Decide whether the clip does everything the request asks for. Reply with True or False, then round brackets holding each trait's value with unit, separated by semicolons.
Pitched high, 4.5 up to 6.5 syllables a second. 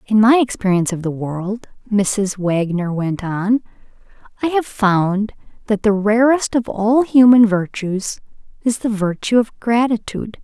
False (215 Hz; 4.3 syllables/s)